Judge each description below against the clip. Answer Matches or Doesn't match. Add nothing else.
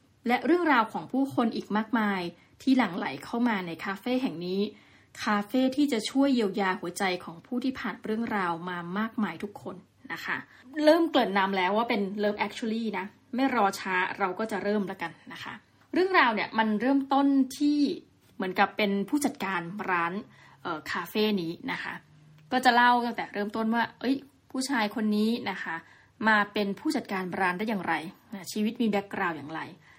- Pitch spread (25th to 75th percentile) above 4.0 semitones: Matches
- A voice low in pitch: Doesn't match